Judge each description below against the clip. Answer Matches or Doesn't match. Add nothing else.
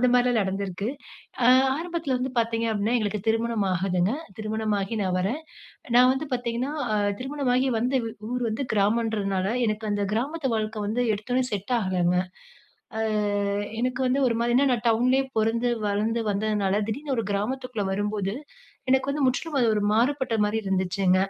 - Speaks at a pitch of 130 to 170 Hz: Doesn't match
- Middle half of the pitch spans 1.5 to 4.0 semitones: Matches